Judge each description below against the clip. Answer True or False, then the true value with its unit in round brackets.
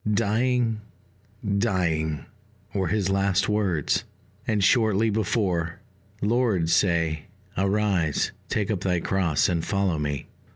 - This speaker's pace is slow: True (110 wpm)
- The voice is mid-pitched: False (95 Hz)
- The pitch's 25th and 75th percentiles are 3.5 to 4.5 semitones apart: True (3.9 semitones)